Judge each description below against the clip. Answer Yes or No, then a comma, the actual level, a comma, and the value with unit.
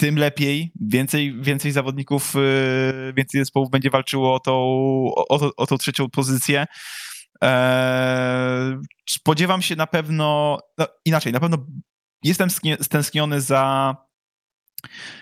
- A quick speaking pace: No, average, 115 wpm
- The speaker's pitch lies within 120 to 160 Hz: Yes, medium, 140 Hz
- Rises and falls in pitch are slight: Yes, narrow, 2.2 semitones